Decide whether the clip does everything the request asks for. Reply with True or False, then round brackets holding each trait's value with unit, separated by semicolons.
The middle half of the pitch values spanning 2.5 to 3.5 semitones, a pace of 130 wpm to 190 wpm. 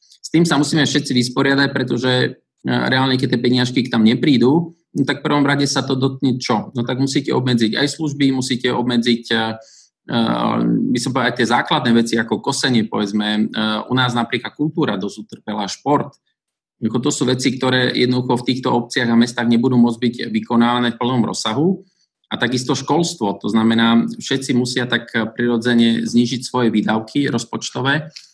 True (2.8 semitones; 165 wpm)